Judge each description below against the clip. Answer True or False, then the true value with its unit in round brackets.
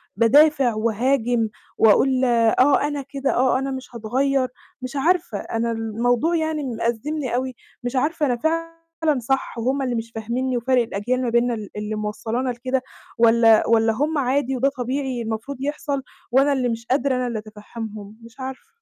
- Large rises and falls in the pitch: False (3.1 semitones)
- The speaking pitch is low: False (250 Hz)